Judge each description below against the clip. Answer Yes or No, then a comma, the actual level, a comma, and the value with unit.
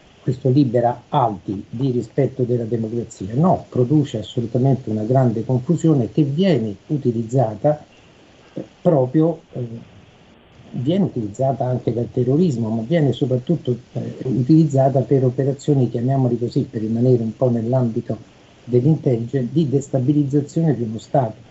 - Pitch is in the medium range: No, low, 130 Hz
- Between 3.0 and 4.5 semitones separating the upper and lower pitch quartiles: Yes, average, 3.4 semitones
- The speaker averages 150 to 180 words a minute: No, average, 120 wpm